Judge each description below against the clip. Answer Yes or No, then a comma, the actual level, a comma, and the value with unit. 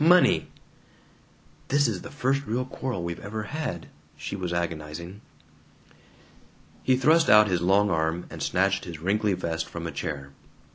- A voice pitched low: Yes, very low, 95 Hz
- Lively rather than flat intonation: Yes, wide, 6.3 semitones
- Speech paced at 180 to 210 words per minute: No, average, 150 wpm